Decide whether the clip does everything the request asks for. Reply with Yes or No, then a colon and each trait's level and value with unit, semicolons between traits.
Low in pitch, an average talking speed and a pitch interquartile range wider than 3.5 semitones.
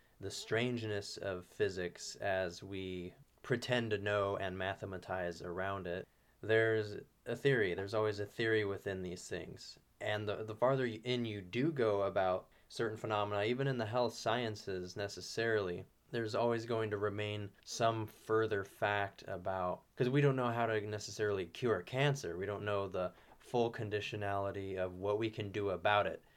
No: low, 105 Hz; average, 160 wpm; narrow, 2.6 semitones